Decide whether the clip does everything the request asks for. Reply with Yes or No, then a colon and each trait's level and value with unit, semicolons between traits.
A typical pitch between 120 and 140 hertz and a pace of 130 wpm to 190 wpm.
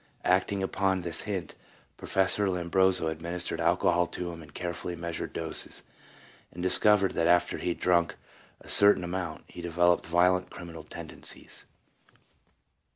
No: very low, 90 Hz; average, 140 wpm